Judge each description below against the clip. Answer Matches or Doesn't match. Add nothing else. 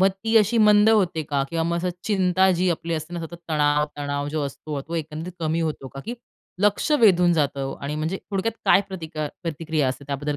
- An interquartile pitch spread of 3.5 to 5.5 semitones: Matches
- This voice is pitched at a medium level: Matches